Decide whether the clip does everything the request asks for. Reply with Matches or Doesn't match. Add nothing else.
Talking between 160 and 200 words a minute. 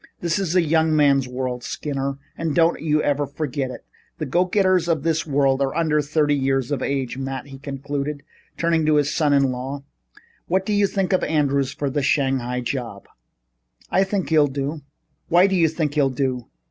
Matches